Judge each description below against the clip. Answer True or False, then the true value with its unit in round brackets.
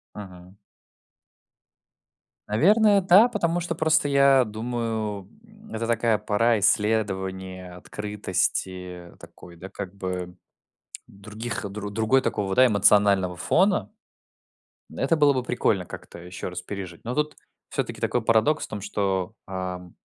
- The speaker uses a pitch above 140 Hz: False (105 Hz)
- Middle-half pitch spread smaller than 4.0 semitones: False (5.2 semitones)